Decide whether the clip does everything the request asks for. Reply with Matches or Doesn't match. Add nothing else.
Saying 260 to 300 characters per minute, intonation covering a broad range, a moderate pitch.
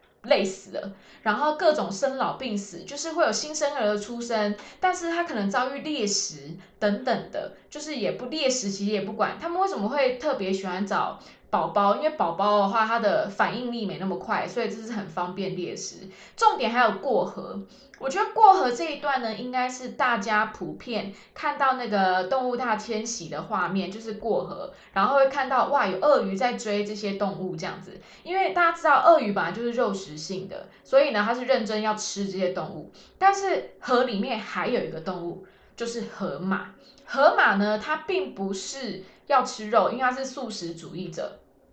Doesn't match